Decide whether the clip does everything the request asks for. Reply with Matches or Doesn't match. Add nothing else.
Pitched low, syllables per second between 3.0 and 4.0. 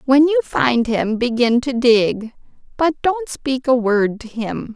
Doesn't match